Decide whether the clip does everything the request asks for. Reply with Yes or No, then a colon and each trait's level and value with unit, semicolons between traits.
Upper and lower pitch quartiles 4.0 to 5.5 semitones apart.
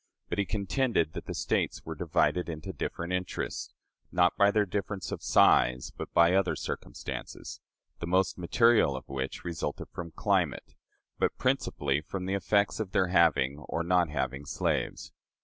Yes: average, 4.4 semitones